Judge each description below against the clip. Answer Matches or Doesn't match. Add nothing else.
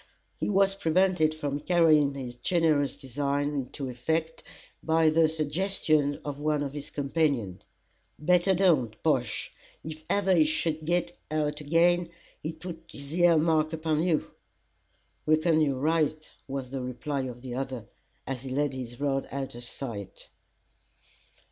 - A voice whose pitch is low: Doesn't match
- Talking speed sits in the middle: Matches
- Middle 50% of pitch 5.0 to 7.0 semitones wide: Doesn't match